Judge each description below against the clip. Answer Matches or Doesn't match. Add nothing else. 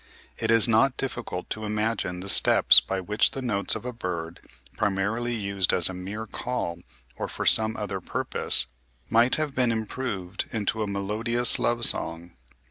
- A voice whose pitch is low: Matches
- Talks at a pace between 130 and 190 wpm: Matches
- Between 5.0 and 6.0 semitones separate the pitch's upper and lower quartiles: Doesn't match